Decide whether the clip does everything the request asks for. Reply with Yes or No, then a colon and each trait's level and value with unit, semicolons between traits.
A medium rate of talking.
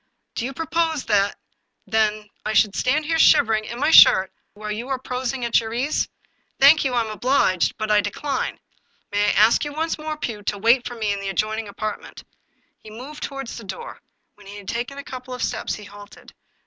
No: fast, 225 wpm